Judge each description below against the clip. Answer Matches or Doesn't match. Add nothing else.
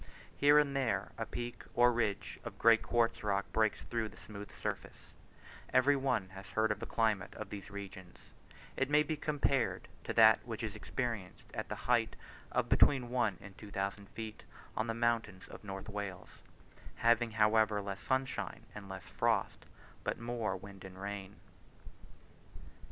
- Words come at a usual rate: Matches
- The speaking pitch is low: Matches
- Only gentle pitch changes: Doesn't match